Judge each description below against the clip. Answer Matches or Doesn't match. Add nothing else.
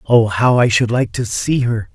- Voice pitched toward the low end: Matches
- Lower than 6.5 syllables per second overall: Matches